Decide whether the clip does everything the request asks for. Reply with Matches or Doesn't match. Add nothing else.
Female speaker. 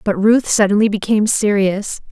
Matches